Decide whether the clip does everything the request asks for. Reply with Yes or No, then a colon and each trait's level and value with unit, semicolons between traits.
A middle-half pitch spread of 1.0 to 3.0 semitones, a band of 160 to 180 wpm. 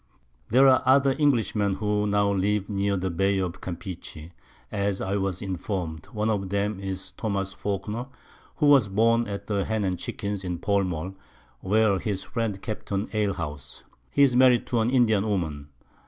Yes: average, 2.7 semitones; average, 170 wpm